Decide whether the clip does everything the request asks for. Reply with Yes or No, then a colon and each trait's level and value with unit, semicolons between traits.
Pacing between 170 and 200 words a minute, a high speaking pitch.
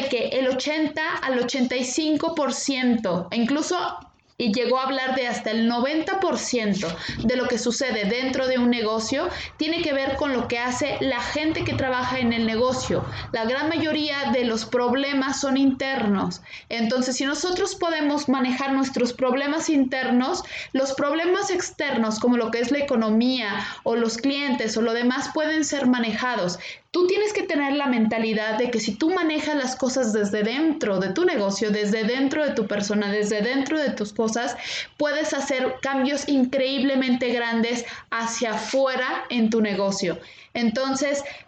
No: average, 160 wpm; very high, 255 Hz